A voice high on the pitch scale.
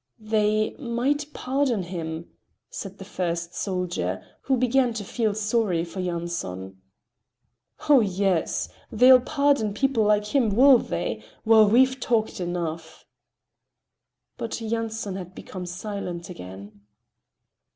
Yes: high, 210 Hz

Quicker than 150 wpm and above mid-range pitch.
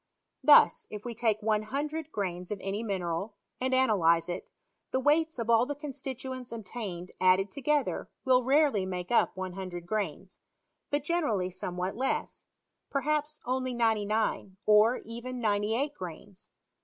No: average, 140 wpm; high, 220 Hz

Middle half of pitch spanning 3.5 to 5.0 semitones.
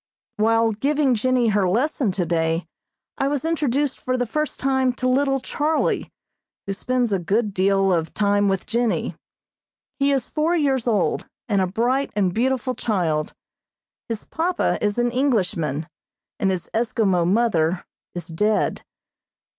No: wide, 5.4 semitones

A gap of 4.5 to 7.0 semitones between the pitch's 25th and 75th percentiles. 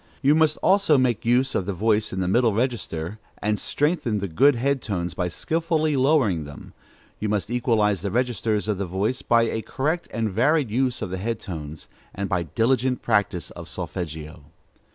Yes: wide, 5.6 semitones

